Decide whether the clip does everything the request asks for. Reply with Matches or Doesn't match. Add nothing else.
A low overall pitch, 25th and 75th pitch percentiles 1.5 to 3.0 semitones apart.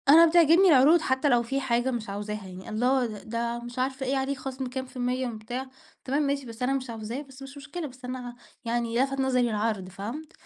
Doesn't match